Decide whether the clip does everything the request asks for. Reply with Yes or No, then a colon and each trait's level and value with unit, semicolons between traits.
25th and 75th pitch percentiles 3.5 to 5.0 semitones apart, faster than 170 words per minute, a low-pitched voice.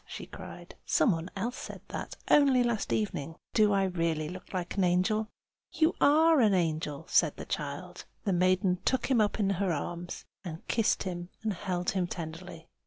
No: average, 4.0 semitones; average, 180 wpm; medium, 185 Hz